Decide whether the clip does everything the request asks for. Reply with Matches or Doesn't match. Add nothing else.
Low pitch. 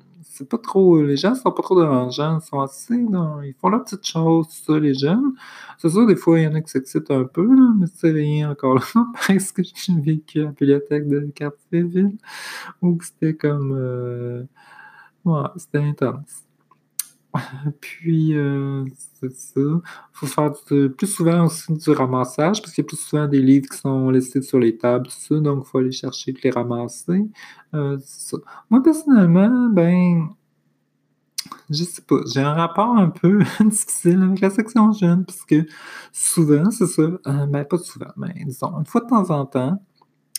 Doesn't match